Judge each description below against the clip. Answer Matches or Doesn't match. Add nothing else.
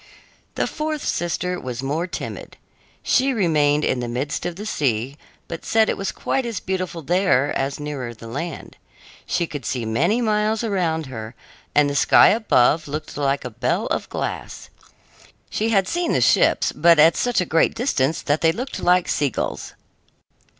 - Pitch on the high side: Doesn't match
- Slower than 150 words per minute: Doesn't match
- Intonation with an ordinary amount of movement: Doesn't match